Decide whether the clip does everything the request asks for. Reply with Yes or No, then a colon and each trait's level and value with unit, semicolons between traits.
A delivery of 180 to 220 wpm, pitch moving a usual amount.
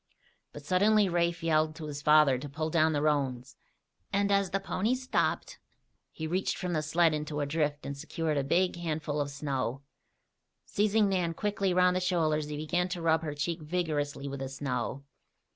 Yes: average, 185 wpm; average, 3.7 semitones